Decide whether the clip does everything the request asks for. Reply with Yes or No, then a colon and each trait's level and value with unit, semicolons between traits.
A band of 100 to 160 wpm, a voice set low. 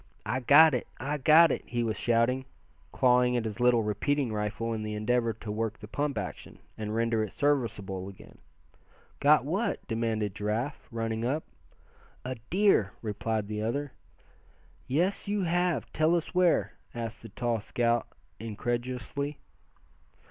Yes: average, 150 wpm; low, 120 Hz